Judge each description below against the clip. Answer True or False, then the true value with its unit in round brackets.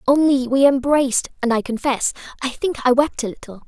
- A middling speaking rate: True (195 wpm)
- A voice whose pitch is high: True (260 Hz)